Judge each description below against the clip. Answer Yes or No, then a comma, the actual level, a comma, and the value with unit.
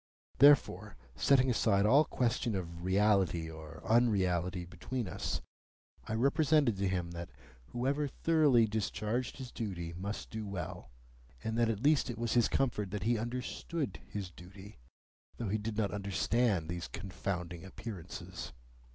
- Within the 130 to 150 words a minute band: Yes, average, 145 wpm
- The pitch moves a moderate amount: Yes, average, 4.9 semitones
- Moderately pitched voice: No, low, 105 Hz